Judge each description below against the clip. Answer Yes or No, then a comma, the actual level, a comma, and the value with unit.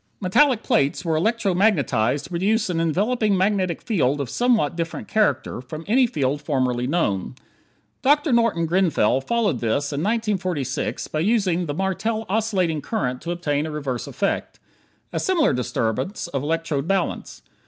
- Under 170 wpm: Yes, average, 155 wpm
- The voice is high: No, medium, 170 Hz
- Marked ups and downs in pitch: Yes, wide, 6.9 semitones